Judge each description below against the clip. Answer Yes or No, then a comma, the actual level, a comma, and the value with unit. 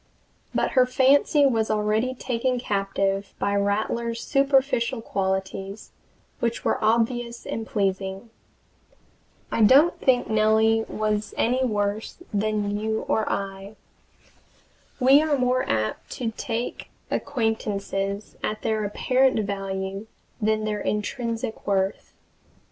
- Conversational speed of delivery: No, slow, 110 wpm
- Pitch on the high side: Yes, high, 220 Hz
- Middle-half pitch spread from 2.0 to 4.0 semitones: Yes, average, 3.4 semitones